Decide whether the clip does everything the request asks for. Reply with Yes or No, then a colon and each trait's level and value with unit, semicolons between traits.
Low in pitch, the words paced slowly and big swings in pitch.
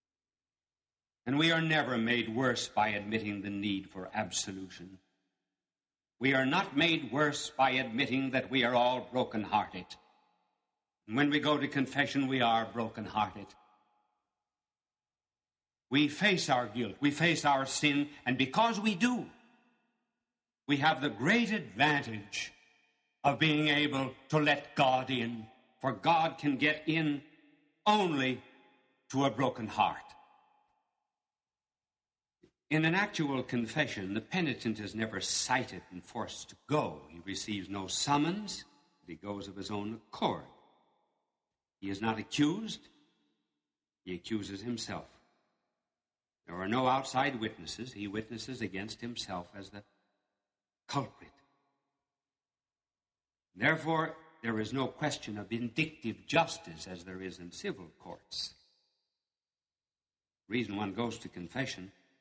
Yes: low, 125 Hz; slow, 125 wpm; wide, 6.2 semitones